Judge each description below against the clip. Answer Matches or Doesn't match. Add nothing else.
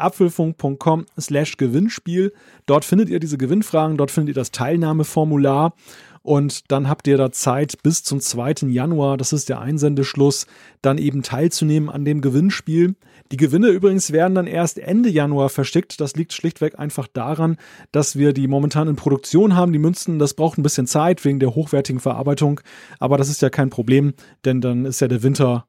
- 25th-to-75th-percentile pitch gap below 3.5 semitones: Matches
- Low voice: Doesn't match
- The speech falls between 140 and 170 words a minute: Doesn't match